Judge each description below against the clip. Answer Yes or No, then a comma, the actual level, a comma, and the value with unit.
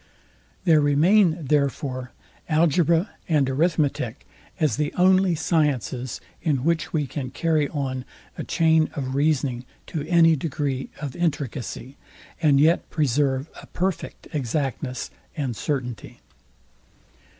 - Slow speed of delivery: Yes, slow, 115 wpm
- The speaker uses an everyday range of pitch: Yes, average, 3.6 semitones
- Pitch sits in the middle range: Yes, medium, 150 Hz